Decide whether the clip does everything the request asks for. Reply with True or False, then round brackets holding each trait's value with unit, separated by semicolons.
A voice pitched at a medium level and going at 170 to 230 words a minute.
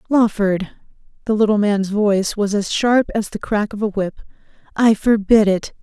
False (210 Hz; 175 wpm)